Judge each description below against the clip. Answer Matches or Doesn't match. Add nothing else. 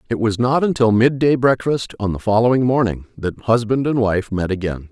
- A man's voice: Matches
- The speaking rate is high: Matches